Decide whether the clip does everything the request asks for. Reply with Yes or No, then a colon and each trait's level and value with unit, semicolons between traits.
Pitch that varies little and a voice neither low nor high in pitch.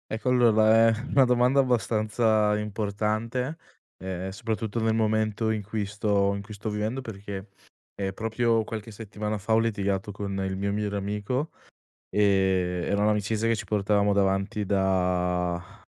No: narrow, 2.1 semitones; low, 105 Hz